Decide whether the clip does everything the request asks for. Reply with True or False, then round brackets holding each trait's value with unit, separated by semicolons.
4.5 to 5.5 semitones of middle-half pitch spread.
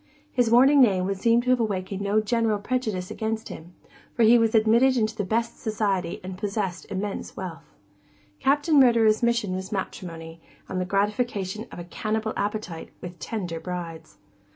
False (3.8 semitones)